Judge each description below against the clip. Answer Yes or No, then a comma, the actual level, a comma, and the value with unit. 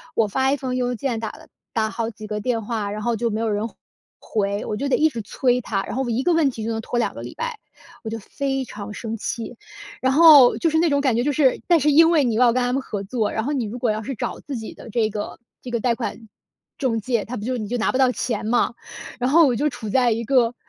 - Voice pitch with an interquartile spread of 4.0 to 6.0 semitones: No, average, 3.3 semitones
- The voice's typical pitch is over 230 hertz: Yes, high, 240 Hz